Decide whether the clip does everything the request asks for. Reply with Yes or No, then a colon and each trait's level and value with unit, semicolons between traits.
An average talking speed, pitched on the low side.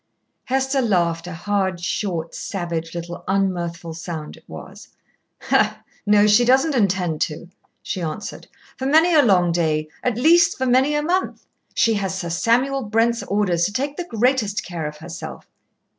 No: average, 160 wpm; high, 200 Hz